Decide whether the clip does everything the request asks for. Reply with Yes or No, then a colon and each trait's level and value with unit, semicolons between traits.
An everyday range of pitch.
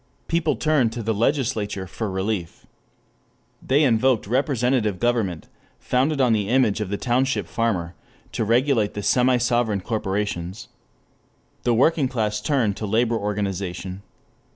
Yes: average, 3.8 semitones